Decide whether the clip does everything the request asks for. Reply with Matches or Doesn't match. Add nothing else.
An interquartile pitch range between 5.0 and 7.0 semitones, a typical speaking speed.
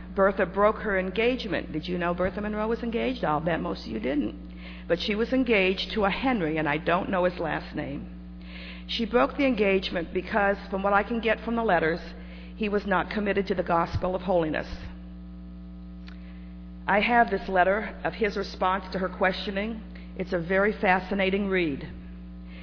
Matches